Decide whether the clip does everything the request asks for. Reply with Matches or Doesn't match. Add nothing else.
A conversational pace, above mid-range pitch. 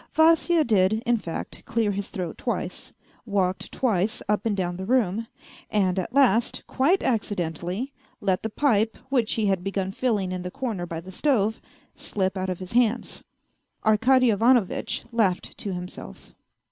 Matches